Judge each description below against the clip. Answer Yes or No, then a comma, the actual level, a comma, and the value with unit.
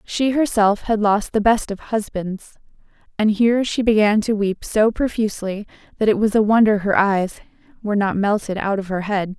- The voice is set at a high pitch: Yes, high, 210 Hz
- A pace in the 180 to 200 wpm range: Yes, average, 190 wpm